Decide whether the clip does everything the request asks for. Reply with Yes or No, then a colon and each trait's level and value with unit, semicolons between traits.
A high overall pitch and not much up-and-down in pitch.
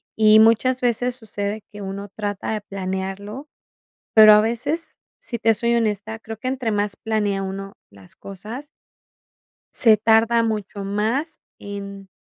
Yes: high, 215 Hz; narrow, 2.3 semitones